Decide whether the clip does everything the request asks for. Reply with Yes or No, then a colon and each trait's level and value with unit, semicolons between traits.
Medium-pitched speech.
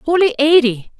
No: very high, 285 Hz